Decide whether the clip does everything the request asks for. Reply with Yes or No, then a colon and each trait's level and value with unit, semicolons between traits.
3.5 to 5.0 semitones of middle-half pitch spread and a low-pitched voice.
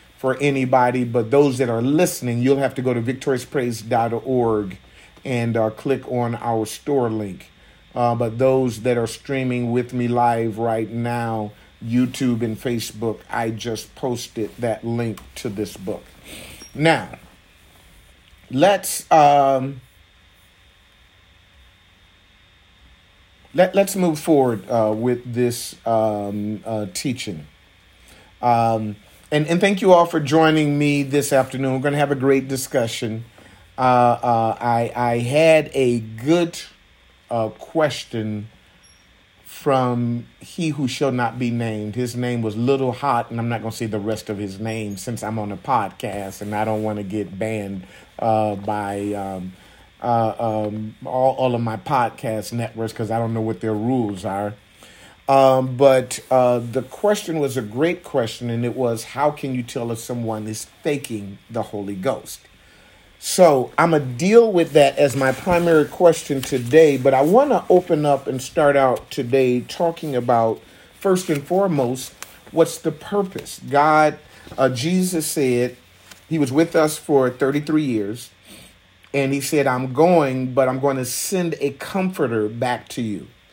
Yes: average, 4.3 semitones; low, 120 Hz